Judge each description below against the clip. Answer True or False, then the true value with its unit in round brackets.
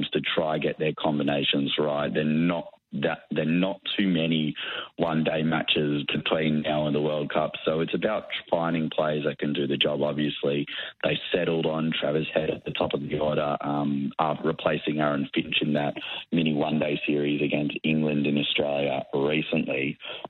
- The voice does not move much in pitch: True (1.4 semitones)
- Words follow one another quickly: False (175 wpm)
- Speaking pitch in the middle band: False (75 Hz)